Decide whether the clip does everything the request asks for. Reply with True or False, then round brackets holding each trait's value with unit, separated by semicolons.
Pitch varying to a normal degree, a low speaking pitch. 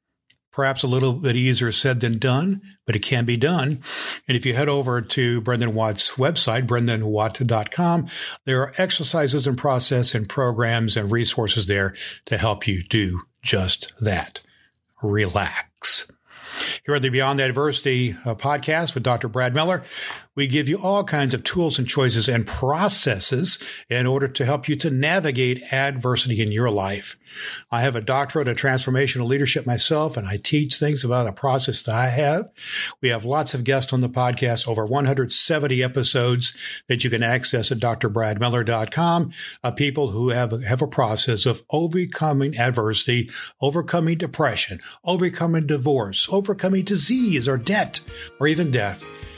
True (3.7 semitones; 130 Hz)